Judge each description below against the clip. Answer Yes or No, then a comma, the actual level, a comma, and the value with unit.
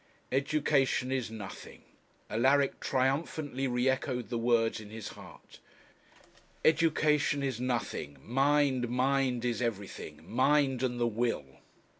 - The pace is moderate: No, slow, 115 wpm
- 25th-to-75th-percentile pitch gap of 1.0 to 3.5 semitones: Yes, average, 2.8 semitones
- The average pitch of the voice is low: Yes, low, 130 Hz